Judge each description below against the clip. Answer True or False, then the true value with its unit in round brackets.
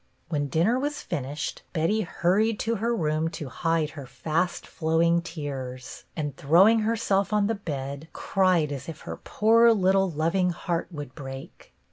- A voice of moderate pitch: True (170 Hz)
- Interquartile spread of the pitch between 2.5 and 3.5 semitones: False (5.1 semitones)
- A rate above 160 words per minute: False (155 wpm)